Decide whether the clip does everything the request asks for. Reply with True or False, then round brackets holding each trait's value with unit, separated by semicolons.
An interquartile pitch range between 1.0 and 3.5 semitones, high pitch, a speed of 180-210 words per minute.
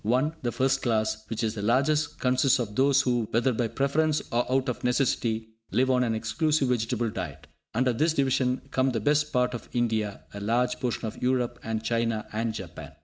False (2.9 semitones; 120 Hz; 200 wpm)